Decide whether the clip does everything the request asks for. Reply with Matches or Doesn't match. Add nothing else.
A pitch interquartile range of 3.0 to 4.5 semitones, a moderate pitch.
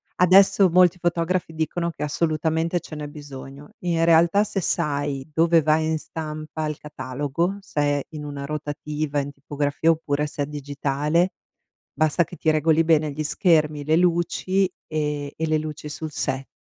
Doesn't match